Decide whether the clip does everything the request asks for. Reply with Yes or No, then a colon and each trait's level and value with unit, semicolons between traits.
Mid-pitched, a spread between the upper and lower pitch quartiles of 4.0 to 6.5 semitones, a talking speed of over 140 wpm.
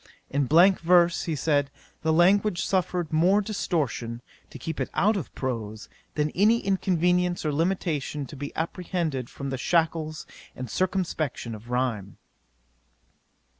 No: medium, 160 Hz; average, 4.7 semitones; slow, 135 wpm